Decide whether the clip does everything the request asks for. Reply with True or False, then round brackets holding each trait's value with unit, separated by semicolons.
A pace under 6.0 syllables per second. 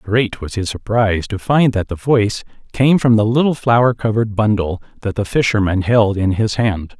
True (5.0 syllables/s)